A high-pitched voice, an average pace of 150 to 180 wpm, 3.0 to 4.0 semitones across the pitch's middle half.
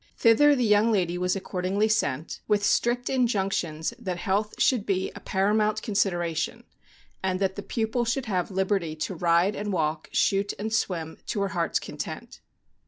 Yes: high, 195 Hz; average, 170 wpm; average, 3.4 semitones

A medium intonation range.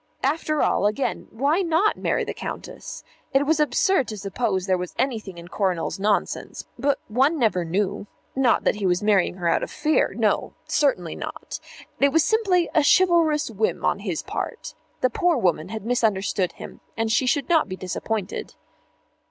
No: wide, 7.6 semitones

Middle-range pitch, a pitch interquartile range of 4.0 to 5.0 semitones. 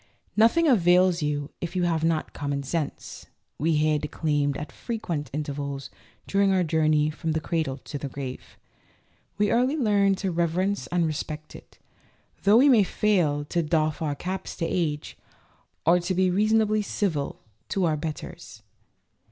Yes: medium, 165 Hz; average, 4.5 semitones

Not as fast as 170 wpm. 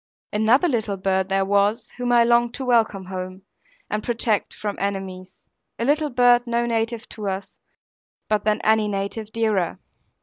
Yes: average, 160 wpm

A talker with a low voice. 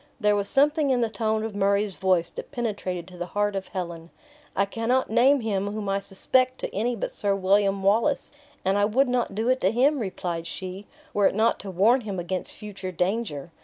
No: high, 205 Hz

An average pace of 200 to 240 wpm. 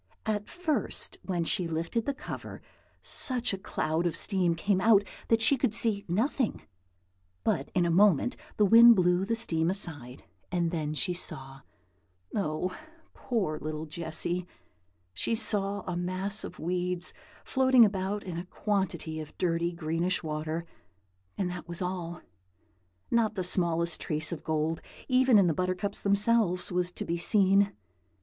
No: average, 150 wpm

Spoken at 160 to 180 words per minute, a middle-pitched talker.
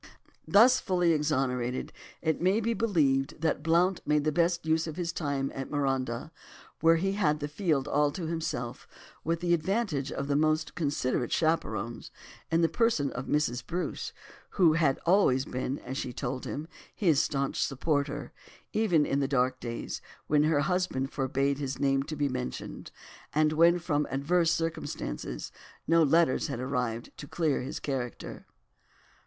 Yes: average, 165 wpm; medium, 150 Hz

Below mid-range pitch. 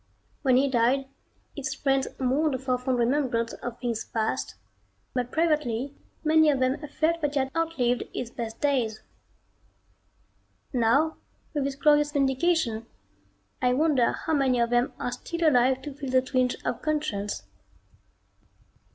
No: very high, 265 Hz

